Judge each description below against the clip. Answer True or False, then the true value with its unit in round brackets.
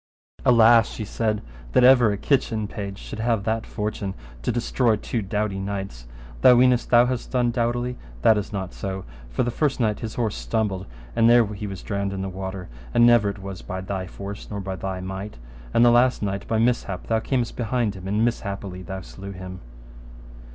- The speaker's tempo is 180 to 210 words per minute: True (200 wpm)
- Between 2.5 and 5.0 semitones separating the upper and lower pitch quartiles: True (3.5 semitones)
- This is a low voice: True (105 Hz)